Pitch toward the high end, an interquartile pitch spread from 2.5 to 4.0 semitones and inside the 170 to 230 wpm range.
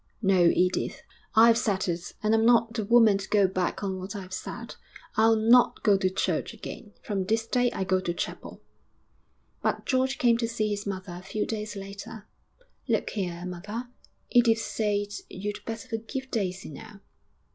Yes: high, 210 Hz; average, 3.0 semitones; average, 175 wpm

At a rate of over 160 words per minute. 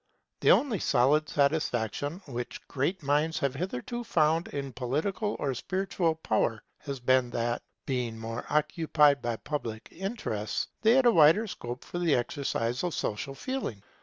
No: average, 150 wpm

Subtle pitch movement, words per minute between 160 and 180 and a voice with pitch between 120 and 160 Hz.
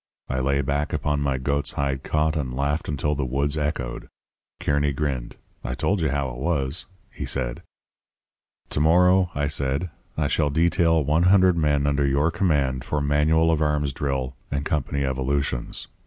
No: narrow, 2.3 semitones; average, 170 wpm; very low, 70 Hz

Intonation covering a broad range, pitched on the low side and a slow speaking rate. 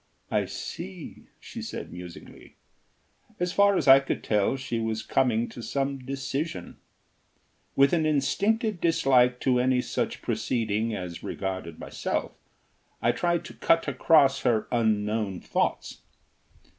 Yes: wide, 5.9 semitones; low, 130 Hz; slow, 130 wpm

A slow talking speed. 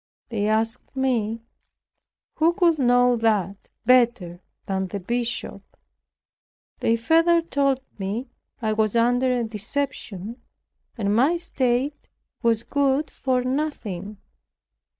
Yes: slow, 110 wpm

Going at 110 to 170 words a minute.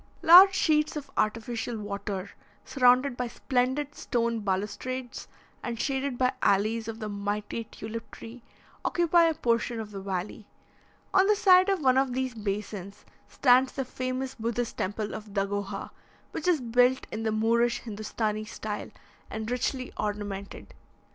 Yes: average, 145 wpm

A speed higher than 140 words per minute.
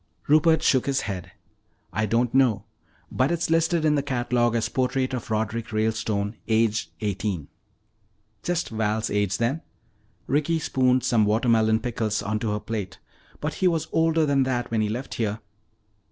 Yes: average, 155 wpm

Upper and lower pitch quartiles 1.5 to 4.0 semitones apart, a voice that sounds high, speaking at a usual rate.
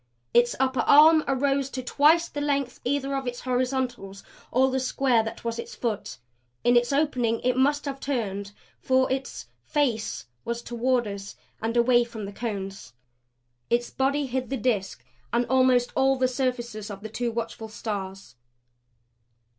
Yes: average, 2.9 semitones; high, 245 Hz; average, 160 wpm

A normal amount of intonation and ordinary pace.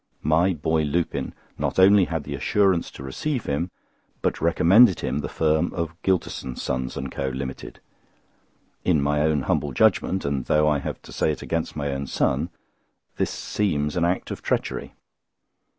Yes: average, 3.7 semitones; average, 165 wpm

